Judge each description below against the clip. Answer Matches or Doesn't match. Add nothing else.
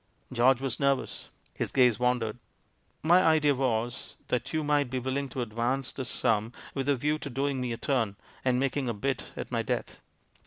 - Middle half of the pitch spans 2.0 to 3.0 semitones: Matches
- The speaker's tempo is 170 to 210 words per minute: Matches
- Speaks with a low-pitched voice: Matches